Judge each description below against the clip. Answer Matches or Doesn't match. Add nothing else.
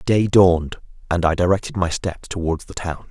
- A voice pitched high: Doesn't match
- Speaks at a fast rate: Doesn't match